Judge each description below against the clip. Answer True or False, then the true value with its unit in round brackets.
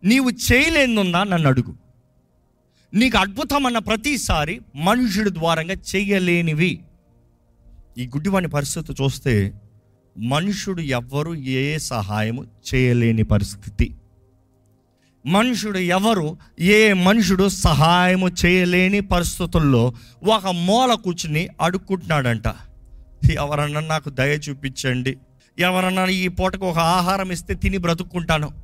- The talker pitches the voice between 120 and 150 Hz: False (165 Hz)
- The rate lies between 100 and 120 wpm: False (90 wpm)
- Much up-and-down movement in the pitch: True (6.9 semitones)